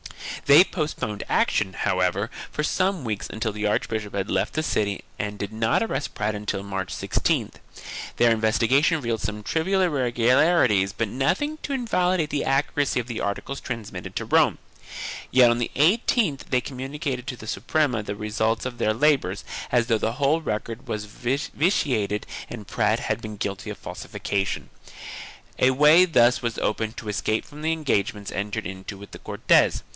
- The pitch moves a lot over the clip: Yes, wide, 5.7 semitones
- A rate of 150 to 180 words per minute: Yes, average, 170 wpm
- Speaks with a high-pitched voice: No, low, 120 Hz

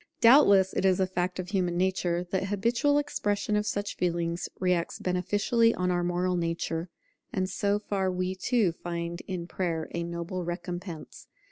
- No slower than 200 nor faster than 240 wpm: No, average, 160 wpm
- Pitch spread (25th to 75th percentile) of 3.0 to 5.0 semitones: No, narrow, 2.5 semitones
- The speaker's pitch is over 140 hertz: Yes, medium, 185 Hz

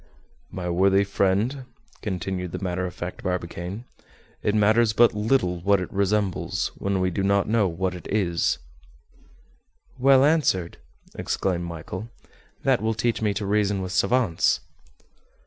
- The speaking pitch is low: Yes, low, 100 Hz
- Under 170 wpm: Yes, average, 140 wpm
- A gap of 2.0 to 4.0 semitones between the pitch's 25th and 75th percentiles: Yes, average, 2.9 semitones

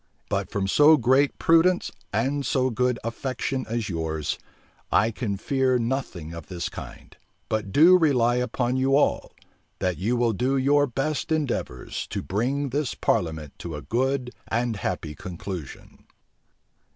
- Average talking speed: Yes, average, 145 wpm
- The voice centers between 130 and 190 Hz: No, low, 120 Hz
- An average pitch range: No, wide, 5.7 semitones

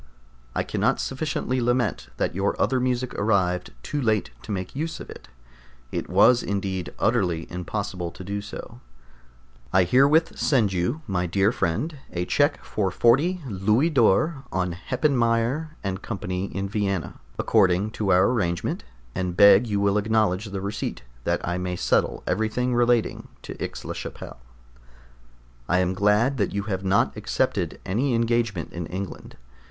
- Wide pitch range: No, average, 4.8 semitones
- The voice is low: Yes, low, 100 Hz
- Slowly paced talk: No, average, 155 wpm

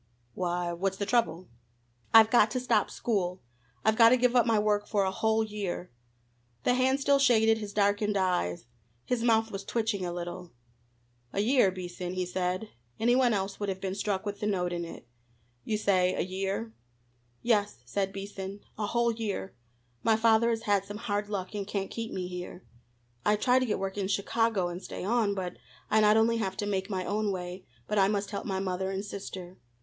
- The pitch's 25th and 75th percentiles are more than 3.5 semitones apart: No, average, 2.8 semitones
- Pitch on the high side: Yes, high, 205 Hz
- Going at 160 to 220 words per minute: Yes, average, 200 wpm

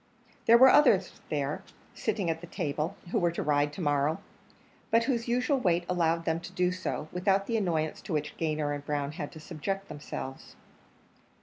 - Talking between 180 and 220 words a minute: Yes, average, 185 wpm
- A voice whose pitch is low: No, medium, 170 Hz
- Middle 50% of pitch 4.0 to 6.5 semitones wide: Yes, average, 4.6 semitones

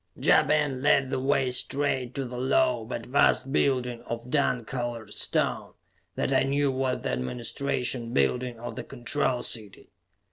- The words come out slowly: No, average, 155 wpm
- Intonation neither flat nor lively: No, narrow, 2.3 semitones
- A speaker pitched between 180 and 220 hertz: No, low, 125 Hz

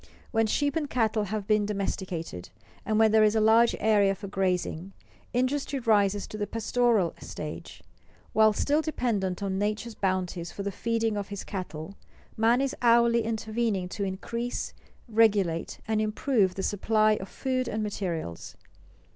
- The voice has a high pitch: Yes, high, 215 Hz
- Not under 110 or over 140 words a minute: No, average, 155 wpm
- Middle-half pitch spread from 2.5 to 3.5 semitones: Yes, average, 3.0 semitones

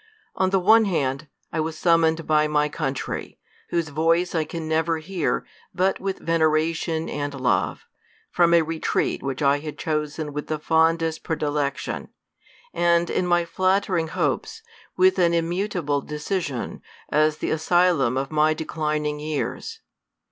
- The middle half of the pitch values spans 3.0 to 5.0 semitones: No, narrow, 2.4 semitones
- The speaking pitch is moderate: Yes, medium, 160 Hz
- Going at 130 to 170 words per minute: Yes, average, 145 wpm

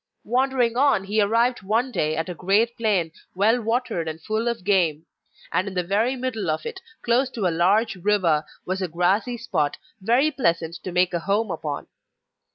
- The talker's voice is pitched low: No, high, 200 Hz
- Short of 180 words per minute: No, average, 185 wpm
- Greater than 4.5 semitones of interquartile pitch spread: Yes, average, 5.2 semitones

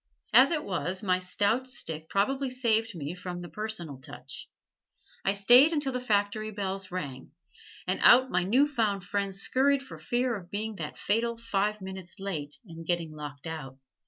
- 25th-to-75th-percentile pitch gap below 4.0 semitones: No, average, 5.1 semitones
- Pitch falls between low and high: No, high, 200 Hz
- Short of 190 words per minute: Yes, average, 170 wpm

